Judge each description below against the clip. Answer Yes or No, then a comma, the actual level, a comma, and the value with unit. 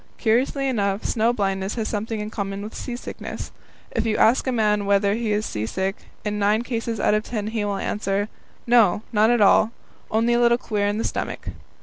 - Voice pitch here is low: No, high, 215 Hz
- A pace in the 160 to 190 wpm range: No, average, 200 wpm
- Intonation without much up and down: Yes, narrow, 2.2 semitones